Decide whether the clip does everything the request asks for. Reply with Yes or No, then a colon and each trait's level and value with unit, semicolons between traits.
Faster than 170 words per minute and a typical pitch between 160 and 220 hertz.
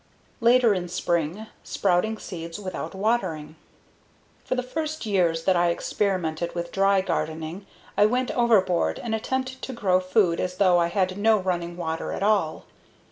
No: average, 155 wpm; high, 190 Hz